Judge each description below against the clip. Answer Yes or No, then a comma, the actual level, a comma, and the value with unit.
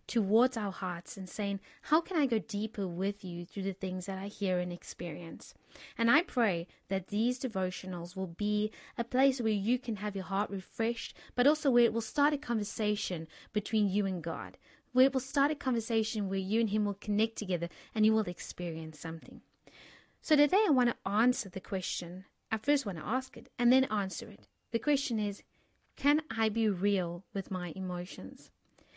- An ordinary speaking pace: Yes, average, 195 wpm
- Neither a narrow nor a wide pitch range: Yes, average, 4.1 semitones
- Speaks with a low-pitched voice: No, high, 210 Hz